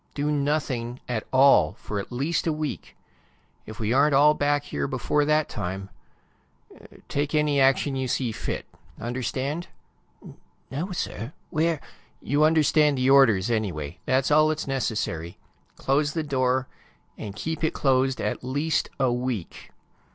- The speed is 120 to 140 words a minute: No, average, 150 wpm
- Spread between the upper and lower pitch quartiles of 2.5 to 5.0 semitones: Yes, average, 3.8 semitones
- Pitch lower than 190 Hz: Yes, low, 135 Hz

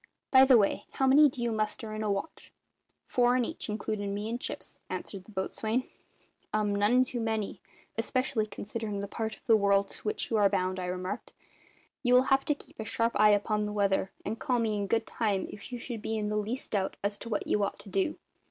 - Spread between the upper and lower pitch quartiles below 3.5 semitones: Yes, narrow, 2.6 semitones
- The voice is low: No, high, 215 Hz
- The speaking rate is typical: No, fast, 230 wpm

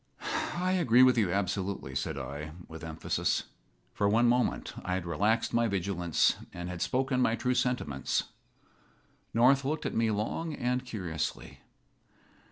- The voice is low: Yes, low, 105 Hz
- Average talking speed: Yes, average, 145 wpm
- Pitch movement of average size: No, wide, 6.2 semitones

